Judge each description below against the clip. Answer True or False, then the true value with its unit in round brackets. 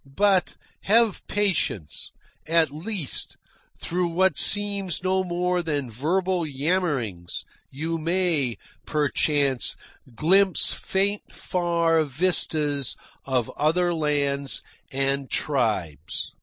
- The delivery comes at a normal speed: False (90 wpm)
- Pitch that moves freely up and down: False (4.8 semitones)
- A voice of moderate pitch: True (165 Hz)